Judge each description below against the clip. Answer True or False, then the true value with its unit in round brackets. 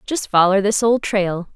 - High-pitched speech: True (205 Hz)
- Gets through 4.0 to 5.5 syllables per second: True (4.2 syllables/s)